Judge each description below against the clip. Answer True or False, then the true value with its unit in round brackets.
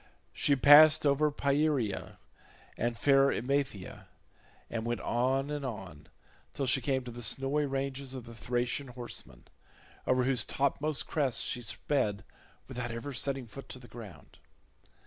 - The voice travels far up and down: False (2.8 semitones)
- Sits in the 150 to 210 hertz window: False (130 Hz)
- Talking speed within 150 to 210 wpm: False (140 wpm)